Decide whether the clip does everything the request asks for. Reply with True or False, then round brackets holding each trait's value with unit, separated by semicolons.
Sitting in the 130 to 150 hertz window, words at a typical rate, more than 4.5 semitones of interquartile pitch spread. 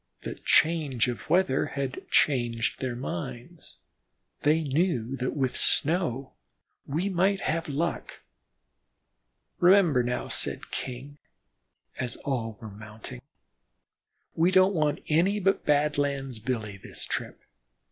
False (140 Hz; 115 wpm; 5.3 semitones)